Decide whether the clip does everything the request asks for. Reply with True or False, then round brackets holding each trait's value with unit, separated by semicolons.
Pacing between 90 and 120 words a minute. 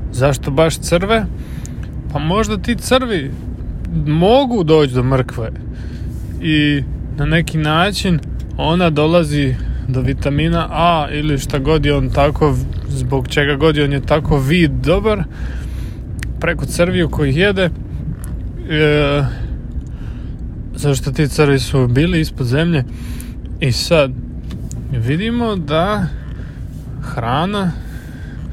True (110 wpm)